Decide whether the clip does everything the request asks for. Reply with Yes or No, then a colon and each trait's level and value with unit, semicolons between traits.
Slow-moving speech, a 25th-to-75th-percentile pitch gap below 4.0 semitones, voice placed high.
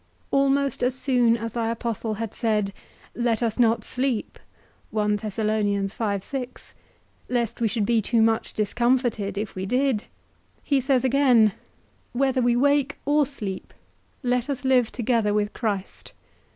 Yes: slow, 130 wpm; average, 3.3 semitones; high, 235 Hz